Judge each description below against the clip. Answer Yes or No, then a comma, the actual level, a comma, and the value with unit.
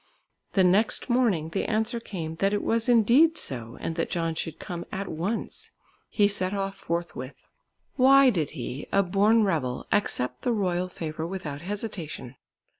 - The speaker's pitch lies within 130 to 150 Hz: No, high, 190 Hz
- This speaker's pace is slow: No, average, 160 wpm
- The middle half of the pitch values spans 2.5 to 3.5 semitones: No, average, 5.0 semitones